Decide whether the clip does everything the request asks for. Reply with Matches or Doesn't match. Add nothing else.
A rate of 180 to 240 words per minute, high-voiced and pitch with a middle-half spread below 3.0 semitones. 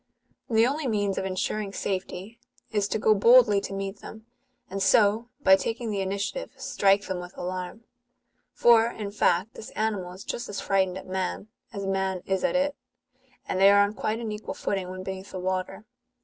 Matches